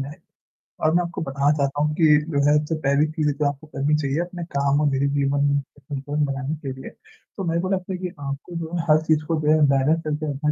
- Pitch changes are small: Yes, narrow, 2.1 semitones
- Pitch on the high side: No, medium, 150 Hz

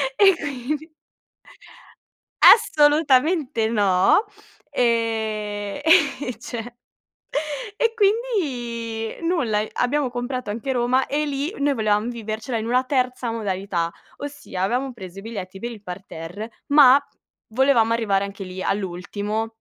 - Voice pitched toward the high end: Yes, high, 235 Hz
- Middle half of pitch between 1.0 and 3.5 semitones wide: No, average, 5.1 semitones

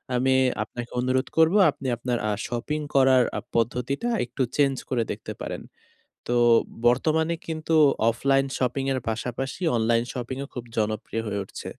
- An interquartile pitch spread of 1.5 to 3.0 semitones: Yes, narrow, 2.5 semitones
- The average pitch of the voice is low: Yes, low, 130 Hz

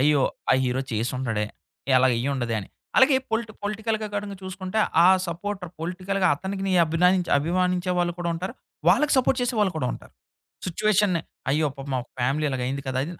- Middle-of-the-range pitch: Yes, medium, 180 Hz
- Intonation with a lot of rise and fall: Yes, wide, 6.6 semitones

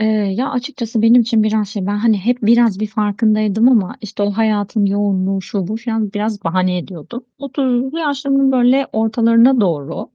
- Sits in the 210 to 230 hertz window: Yes, high, 220 Hz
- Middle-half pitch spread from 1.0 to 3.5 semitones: Yes, average, 3.1 semitones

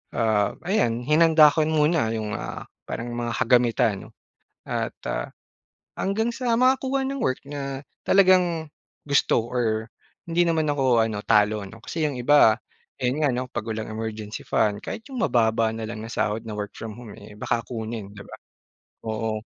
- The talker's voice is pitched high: No, low, 120 Hz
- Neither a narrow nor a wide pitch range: No, wide, 6.1 semitones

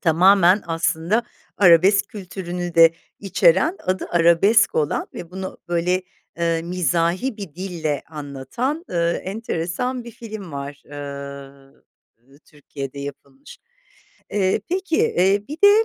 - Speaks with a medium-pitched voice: Yes, medium, 175 Hz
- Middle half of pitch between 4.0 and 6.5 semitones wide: Yes, average, 4.4 semitones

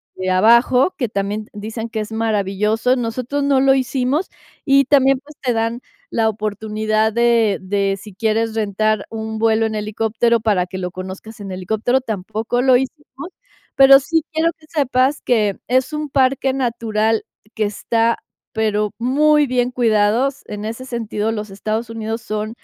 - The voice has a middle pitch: No, high, 225 Hz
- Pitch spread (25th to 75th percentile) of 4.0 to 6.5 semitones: No, average, 3.3 semitones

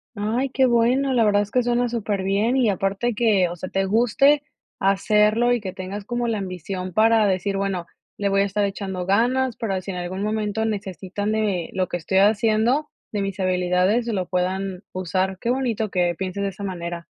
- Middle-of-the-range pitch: No, high, 200 Hz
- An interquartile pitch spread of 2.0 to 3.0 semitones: No, average, 3.4 semitones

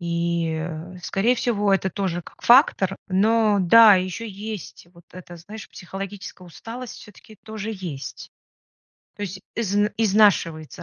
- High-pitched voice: Yes, high, 195 Hz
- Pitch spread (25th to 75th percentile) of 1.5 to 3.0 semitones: No, average, 3.7 semitones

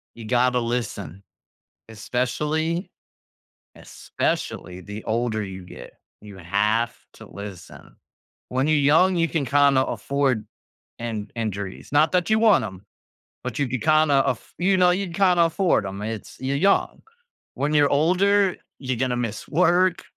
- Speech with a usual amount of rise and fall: No, wide, 7.1 semitones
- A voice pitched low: Yes, low, 130 Hz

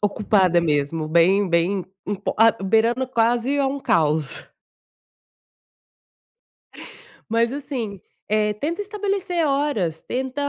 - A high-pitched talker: Yes, high, 220 Hz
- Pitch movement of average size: No, wide, 7.3 semitones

